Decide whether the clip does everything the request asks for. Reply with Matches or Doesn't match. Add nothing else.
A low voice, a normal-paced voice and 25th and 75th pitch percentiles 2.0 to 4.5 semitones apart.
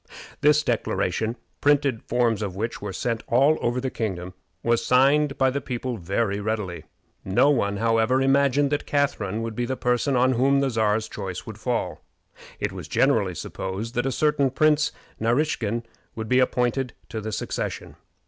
Matches